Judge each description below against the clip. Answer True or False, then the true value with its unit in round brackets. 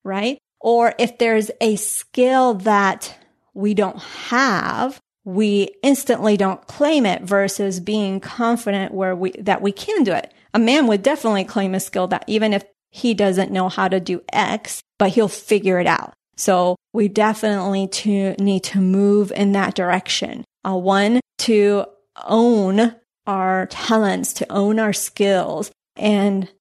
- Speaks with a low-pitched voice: False (200 Hz)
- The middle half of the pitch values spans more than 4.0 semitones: False (2.4 semitones)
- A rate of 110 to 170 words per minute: True (155 wpm)